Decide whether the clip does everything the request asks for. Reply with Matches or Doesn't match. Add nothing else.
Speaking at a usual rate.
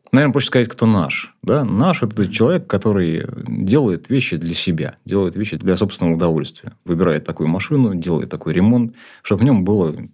Doesn't match